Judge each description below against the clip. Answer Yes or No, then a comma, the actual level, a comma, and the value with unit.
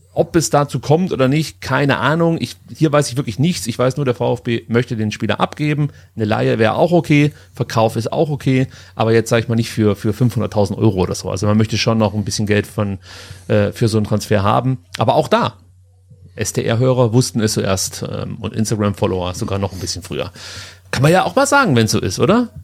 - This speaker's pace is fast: Yes, fast, 225 wpm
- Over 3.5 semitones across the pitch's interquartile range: Yes, average, 4.0 semitones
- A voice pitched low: Yes, low, 115 Hz